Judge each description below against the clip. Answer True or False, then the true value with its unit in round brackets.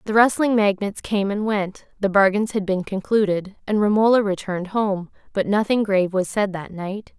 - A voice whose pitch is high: True (200 Hz)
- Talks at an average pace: True (185 wpm)